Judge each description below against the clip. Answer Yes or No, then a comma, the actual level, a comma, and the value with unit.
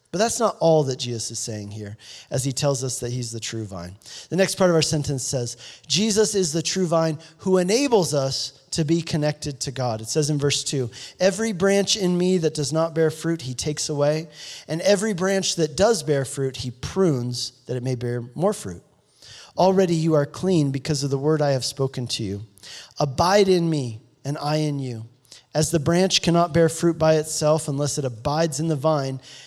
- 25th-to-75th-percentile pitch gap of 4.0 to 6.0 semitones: Yes, average, 4.4 semitones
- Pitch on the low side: No, medium, 150 Hz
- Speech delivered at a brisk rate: Yes, fast, 210 wpm